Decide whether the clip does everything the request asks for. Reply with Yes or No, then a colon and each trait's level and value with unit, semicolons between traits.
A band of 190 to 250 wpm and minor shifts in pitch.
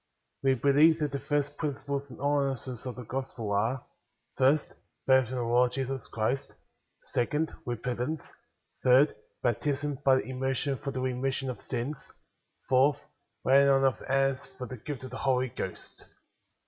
No: average, 165 wpm; narrow, 1.8 semitones